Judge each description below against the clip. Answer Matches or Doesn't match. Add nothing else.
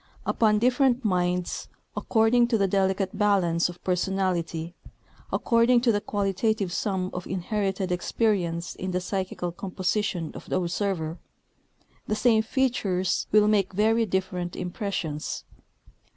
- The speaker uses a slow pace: Matches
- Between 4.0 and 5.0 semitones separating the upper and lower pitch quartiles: Doesn't match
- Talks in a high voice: Matches